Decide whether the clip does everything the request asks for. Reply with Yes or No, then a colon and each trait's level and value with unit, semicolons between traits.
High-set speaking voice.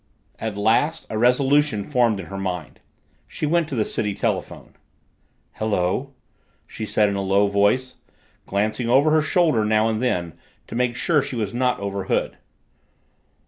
No: low, 110 Hz